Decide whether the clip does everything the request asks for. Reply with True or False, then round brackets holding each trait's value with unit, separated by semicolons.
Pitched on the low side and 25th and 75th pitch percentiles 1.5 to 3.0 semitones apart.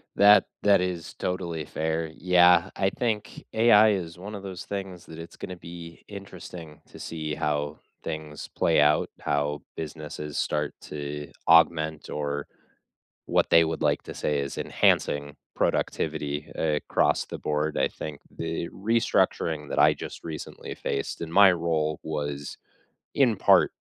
False (80 Hz; 3.4 semitones)